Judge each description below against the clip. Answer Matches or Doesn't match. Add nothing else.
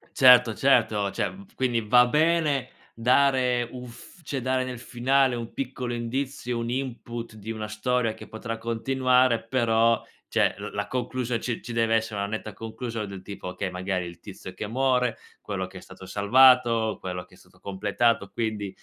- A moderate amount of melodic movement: Matches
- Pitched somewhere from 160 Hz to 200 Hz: Doesn't match